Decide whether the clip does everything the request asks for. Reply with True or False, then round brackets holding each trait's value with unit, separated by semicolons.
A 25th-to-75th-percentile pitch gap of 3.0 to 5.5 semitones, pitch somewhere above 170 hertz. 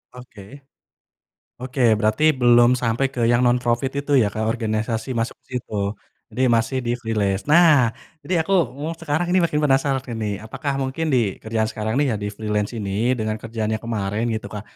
False (3.6 semitones; 120 Hz)